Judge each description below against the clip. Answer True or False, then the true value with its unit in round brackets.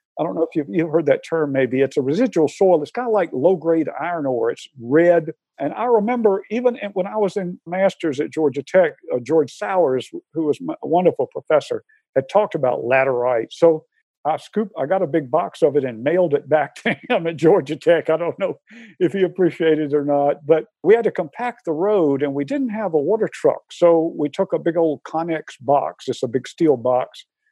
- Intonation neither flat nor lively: False (5.7 semitones)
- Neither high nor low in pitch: True (165 Hz)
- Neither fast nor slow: False (225 wpm)